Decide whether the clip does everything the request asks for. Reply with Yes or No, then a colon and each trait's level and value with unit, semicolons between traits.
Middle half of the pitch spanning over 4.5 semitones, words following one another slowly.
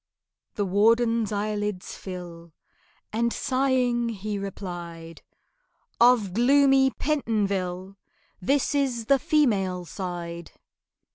Yes: average, 5.0 semitones; slow, 85 wpm